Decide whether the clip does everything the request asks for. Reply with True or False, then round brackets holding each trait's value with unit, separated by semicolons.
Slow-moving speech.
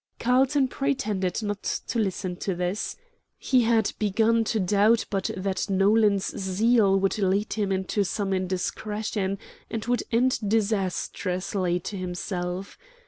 True (130 wpm)